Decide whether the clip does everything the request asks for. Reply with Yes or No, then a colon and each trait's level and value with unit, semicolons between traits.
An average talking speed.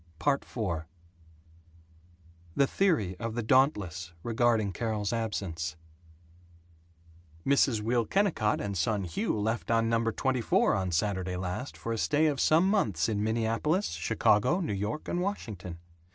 No: slow, 130 wpm